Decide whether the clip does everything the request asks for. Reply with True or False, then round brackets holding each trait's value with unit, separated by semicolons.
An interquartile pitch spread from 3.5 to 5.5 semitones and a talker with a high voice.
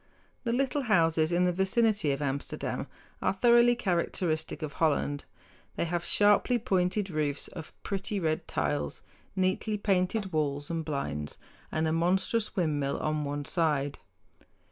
False (4.9 semitones; 170 Hz)